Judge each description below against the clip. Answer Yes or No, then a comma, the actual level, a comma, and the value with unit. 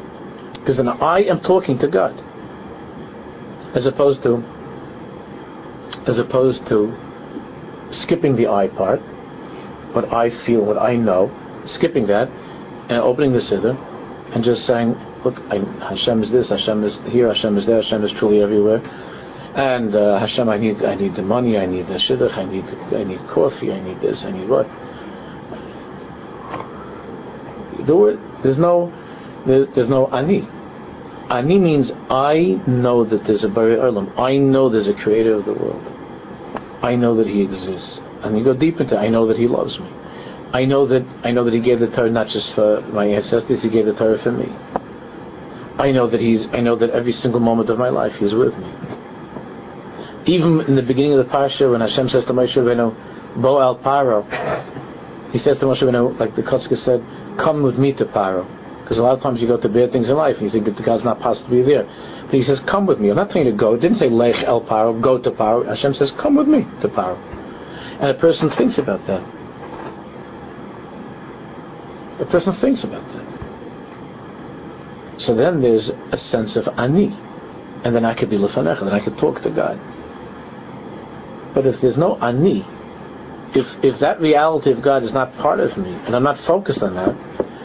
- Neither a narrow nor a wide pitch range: Yes, average, 3.6 semitones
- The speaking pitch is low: Yes, low, 120 Hz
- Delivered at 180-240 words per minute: Yes, average, 190 wpm